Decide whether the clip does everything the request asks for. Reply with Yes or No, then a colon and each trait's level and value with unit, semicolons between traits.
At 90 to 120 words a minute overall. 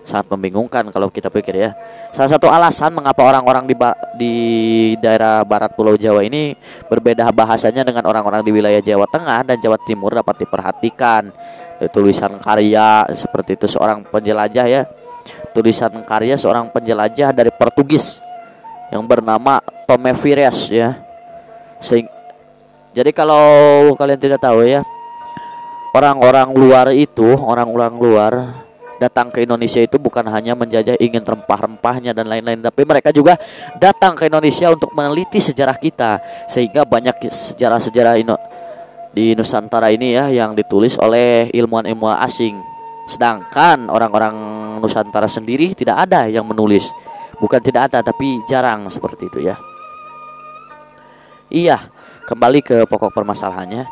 No: average, 130 wpm